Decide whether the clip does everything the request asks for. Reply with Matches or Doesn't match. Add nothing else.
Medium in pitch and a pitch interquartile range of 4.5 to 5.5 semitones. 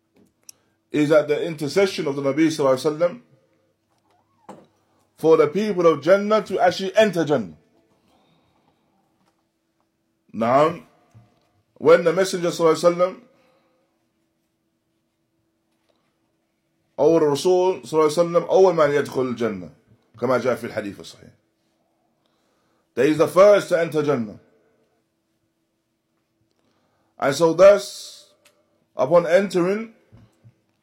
Matches